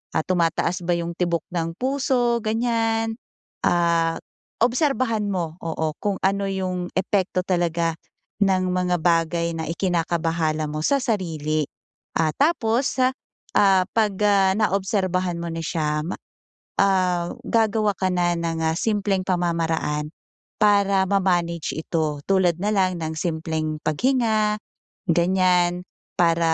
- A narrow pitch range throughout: No, average, 3.5 semitones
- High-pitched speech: No, medium, 180 Hz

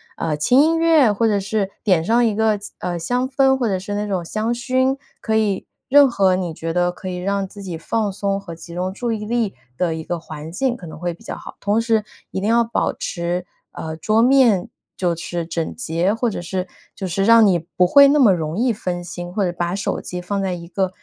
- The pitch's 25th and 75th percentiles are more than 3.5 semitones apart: Yes, average, 4.5 semitones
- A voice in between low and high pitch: No, high, 195 Hz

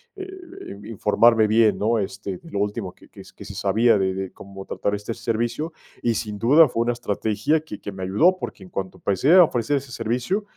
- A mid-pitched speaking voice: No, low, 115 Hz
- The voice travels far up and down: Yes, wide, 5.9 semitones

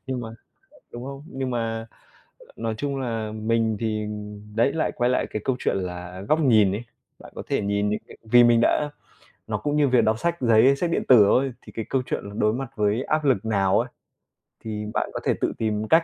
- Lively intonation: No, average, 3.7 semitones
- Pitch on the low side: Yes, low, 115 Hz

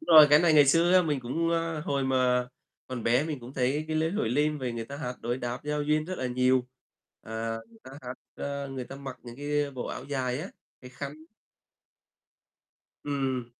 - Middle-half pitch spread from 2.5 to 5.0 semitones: Yes, average, 3.2 semitones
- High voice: No, low, 135 Hz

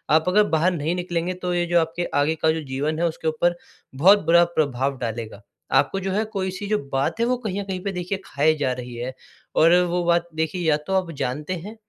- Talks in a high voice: No, medium, 170 Hz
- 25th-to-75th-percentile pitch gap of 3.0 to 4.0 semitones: Yes, average, 3.4 semitones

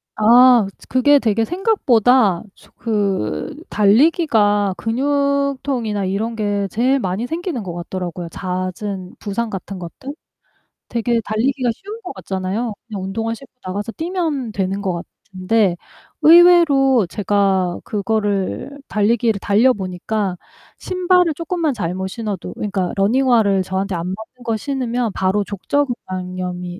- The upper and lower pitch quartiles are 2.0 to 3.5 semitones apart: No, average, 5.2 semitones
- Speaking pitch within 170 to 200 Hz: No, high, 215 Hz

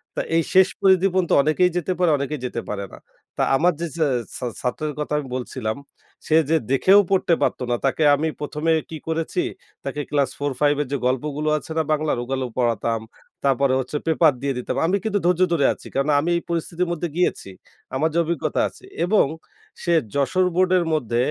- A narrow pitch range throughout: No, average, 4.1 semitones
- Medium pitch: Yes, medium, 150 Hz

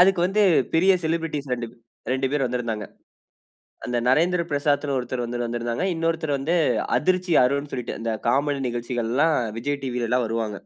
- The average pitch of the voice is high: No, low, 135 Hz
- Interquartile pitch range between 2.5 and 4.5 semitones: No, average, 5.0 semitones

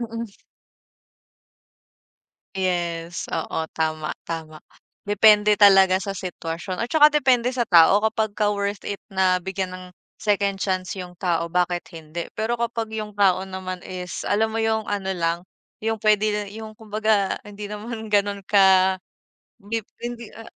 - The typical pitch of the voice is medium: No, high, 200 Hz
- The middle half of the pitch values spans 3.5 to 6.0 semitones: No, average, 3.0 semitones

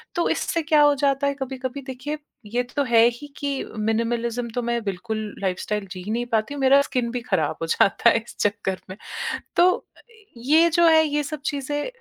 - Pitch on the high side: Yes, very high, 250 Hz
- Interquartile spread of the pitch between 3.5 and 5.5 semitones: Yes, average, 4.4 semitones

